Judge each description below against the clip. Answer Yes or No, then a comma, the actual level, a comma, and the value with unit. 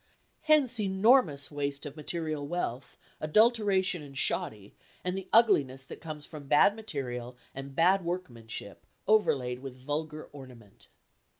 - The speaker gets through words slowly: Yes, slow, 125 wpm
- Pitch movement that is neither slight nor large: No, wide, 6.1 semitones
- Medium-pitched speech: Yes, medium, 150 Hz